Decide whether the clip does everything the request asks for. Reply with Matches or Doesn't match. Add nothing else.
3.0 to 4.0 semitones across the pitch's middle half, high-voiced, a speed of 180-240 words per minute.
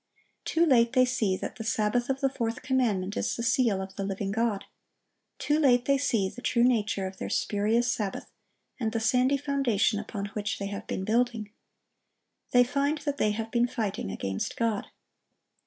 Matches